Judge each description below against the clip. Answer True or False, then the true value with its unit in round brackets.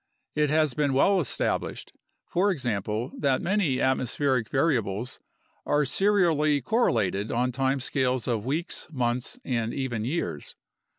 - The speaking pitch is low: True (130 Hz)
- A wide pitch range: False (4.1 semitones)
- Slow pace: True (130 wpm)